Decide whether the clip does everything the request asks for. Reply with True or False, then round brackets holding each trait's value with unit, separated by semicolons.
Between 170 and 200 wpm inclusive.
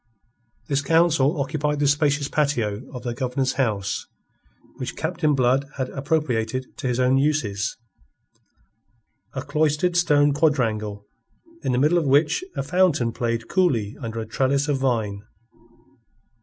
False (135 wpm)